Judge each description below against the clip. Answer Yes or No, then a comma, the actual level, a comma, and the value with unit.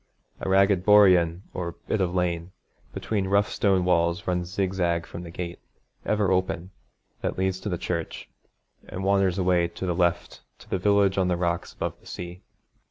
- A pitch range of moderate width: No, narrow, 1.8 semitones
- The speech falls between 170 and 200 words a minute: Yes, average, 175 wpm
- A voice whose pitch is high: No, very low, 90 Hz